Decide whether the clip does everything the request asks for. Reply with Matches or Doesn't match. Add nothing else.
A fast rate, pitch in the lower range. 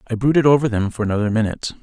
Matches